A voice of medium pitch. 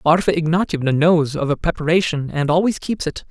Yes: medium, 160 Hz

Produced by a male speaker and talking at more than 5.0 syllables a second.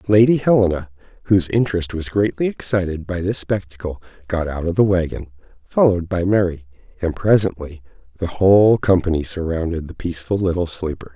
Yes: male; 5.8 syllables/s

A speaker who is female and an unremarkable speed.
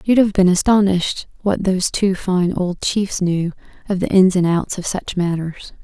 Yes: female; average, 195 wpm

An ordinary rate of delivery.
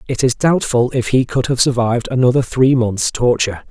Yes: average, 195 wpm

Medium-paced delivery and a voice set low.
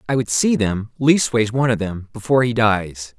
Yes: average, 190 wpm; low, 115 Hz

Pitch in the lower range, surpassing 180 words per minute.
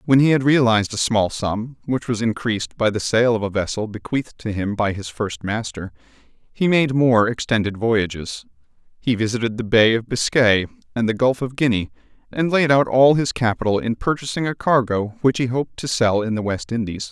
Yes: low, 115 Hz; fast, 205 wpm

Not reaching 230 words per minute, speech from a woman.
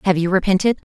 Yes: average, 200 wpm; female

